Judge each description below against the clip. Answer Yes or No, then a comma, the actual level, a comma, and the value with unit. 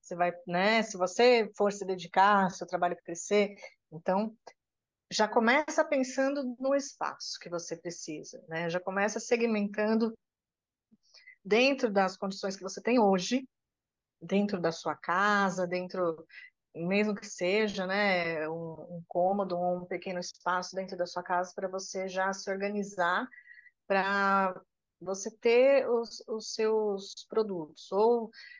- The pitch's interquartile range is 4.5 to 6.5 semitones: No, average, 3.8 semitones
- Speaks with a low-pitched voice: No, high, 195 Hz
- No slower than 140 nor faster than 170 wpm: No, average, 130 wpm